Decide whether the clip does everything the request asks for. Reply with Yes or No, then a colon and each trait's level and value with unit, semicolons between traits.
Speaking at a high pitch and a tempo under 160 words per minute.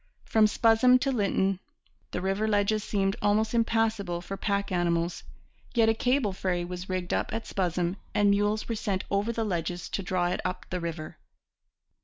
No: high, 200 Hz; average, 175 wpm